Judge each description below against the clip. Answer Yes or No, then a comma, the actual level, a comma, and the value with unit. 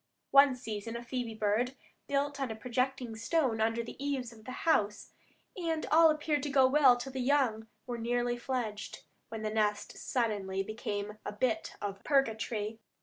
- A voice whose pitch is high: Yes, high, 240 Hz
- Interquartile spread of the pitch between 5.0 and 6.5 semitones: No, average, 3.7 semitones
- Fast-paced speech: No, average, 170 wpm